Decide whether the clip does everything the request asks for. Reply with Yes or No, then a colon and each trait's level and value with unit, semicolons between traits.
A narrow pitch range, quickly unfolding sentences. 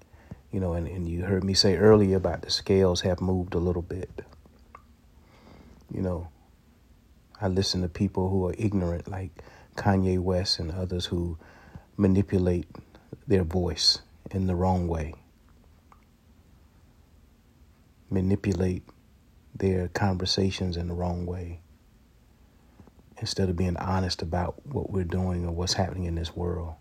No: narrow, 2.2 semitones; slow, 135 wpm